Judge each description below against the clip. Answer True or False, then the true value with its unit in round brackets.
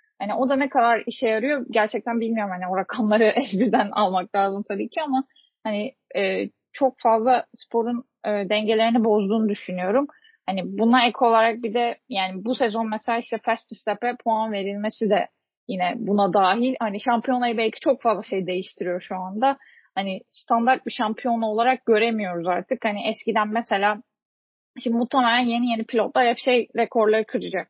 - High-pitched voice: True (225 Hz)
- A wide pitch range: False (2.6 semitones)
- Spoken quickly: True (160 wpm)